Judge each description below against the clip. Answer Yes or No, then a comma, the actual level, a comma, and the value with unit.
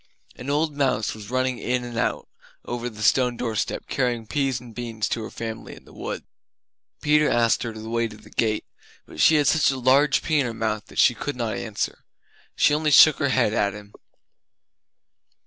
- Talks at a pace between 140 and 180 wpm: No, average, 200 wpm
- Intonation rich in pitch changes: No, average, 3.6 semitones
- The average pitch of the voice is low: Yes, low, 120 Hz